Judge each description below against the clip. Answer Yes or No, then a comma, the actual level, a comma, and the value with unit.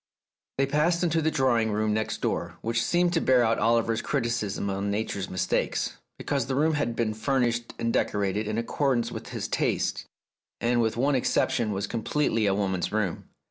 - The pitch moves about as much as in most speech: Yes, average, 4.1 semitones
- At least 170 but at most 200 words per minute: Yes, average, 180 wpm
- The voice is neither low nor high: No, low, 115 Hz